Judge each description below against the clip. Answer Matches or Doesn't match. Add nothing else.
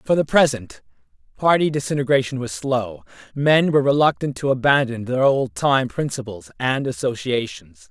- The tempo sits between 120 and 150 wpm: Matches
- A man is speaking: Matches